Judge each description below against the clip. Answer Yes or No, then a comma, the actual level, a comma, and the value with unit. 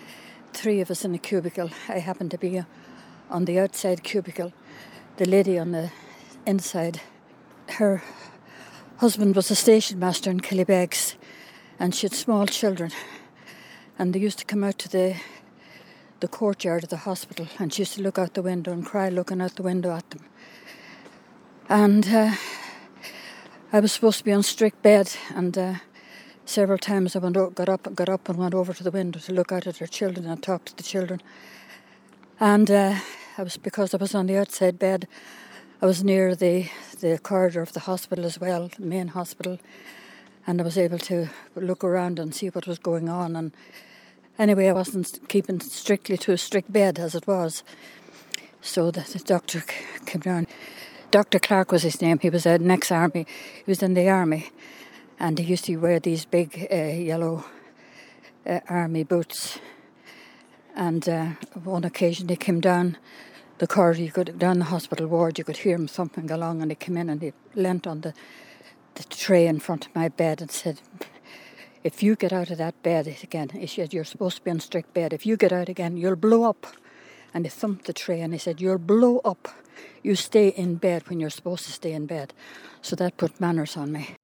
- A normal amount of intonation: No, narrow, 2.3 semitones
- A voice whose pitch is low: No, medium, 180 Hz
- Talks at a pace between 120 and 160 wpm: No, average, 195 wpm